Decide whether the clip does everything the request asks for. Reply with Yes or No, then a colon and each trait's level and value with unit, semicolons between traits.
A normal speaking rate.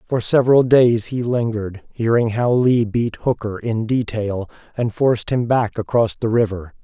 Yes: average, 165 wpm